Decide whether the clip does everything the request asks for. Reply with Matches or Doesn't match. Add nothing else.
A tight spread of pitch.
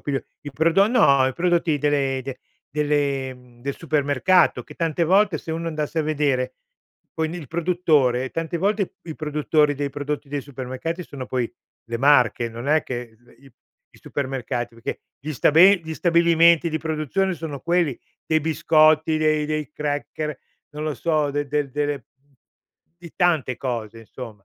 Doesn't match